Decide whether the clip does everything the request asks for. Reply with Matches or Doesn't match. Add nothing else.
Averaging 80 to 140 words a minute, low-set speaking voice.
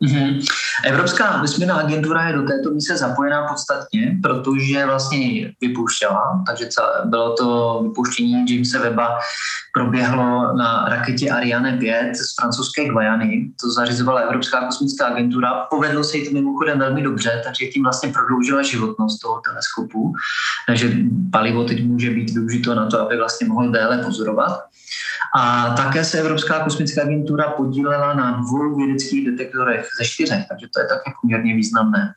Doesn't match